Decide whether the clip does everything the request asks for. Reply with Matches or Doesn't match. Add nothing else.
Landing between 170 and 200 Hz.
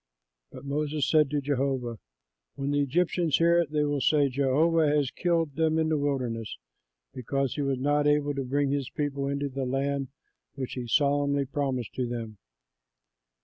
Doesn't match